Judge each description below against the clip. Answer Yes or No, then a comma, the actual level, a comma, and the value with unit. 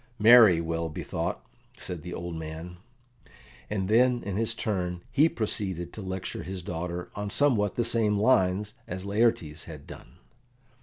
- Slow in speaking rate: No, average, 150 wpm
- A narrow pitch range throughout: No, average, 3.9 semitones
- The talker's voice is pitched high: No, very low, 95 Hz